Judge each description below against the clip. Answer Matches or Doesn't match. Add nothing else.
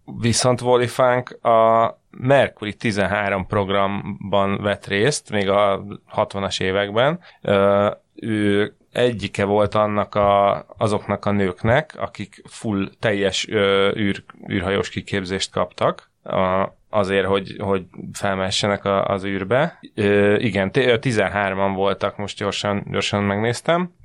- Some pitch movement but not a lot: Doesn't match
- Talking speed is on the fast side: Doesn't match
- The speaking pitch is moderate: Doesn't match